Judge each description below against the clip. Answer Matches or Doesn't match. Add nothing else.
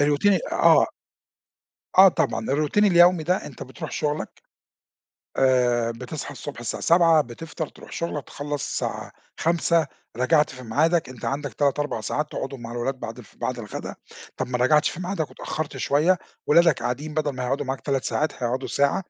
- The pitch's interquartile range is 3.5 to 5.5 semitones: Matches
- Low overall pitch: Doesn't match